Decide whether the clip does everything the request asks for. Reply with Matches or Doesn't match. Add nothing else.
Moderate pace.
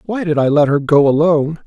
Doesn't match